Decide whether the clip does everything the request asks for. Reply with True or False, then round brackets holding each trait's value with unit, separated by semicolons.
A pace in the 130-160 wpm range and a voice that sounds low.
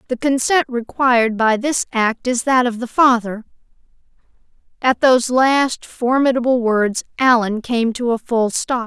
False (150 wpm; 245 Hz)